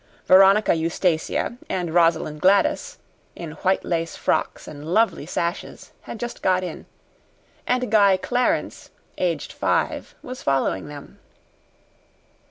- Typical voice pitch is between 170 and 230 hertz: Yes, medium, 185 Hz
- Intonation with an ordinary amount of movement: Yes, average, 4.5 semitones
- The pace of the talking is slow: Yes, slow, 115 wpm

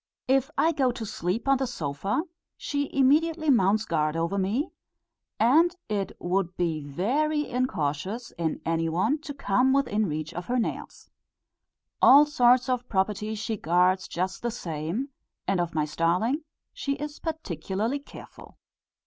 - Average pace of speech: Yes, average, 150 wpm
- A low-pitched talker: No, high, 220 Hz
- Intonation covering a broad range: Yes, wide, 7.7 semitones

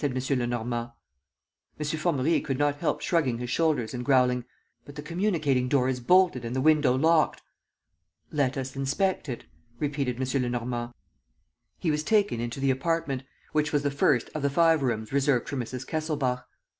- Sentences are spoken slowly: No, average, 165 wpm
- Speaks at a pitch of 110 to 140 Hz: Yes, low, 135 Hz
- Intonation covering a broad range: No, average, 3.3 semitones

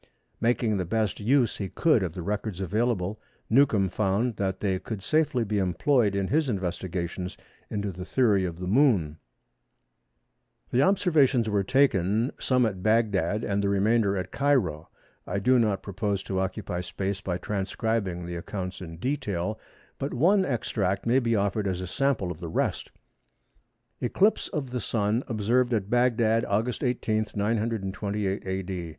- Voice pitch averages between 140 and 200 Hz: No, low, 105 Hz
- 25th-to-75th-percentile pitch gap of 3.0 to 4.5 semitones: Yes, average, 4.2 semitones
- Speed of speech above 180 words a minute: No, average, 155 wpm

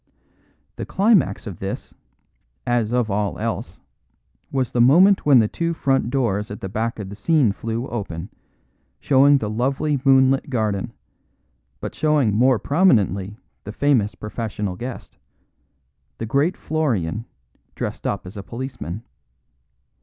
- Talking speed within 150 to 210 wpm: No, slow, 135 wpm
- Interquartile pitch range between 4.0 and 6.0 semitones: Yes, average, 4.9 semitones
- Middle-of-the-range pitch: No, low, 120 Hz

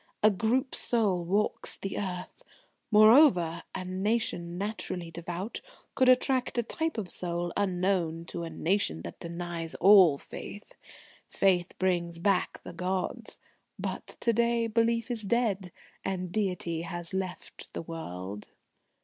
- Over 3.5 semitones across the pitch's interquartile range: Yes, average, 4.0 semitones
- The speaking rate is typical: No, slow, 130 wpm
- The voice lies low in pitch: No, medium, 185 Hz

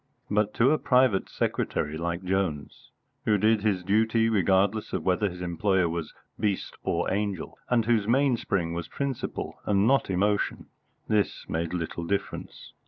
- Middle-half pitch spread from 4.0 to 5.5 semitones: No, average, 3.6 semitones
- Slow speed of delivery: No, average, 150 wpm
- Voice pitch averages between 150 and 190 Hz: No, low, 100 Hz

